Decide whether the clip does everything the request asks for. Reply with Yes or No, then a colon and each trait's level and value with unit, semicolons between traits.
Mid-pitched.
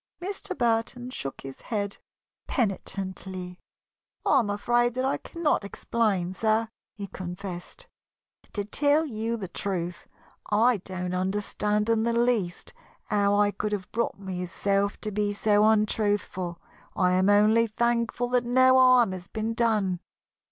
No: high, 210 Hz